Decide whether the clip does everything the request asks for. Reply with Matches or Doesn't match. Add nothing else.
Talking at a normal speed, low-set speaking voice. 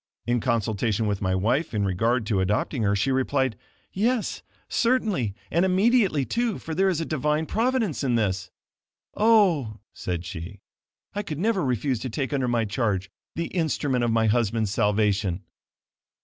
Matches